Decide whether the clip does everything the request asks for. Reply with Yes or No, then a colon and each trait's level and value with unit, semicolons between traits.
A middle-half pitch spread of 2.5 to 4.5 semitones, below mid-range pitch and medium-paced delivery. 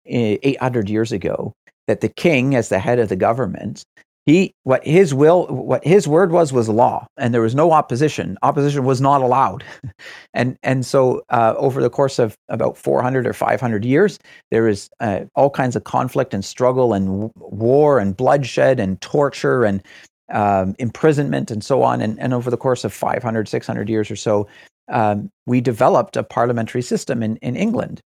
Yes: average, 3.8 semitones; low, 125 Hz; average, 185 wpm